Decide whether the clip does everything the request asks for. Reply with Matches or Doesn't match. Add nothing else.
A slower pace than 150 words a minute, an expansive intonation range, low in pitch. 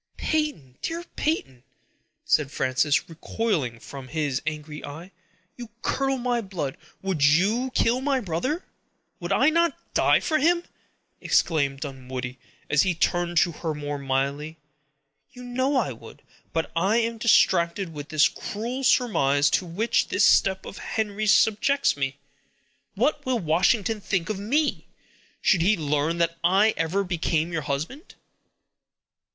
Doesn't match